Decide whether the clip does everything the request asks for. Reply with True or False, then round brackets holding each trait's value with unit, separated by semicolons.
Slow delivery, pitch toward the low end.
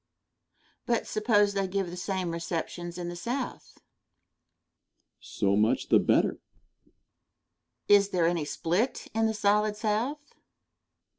False (130 wpm; 200 Hz)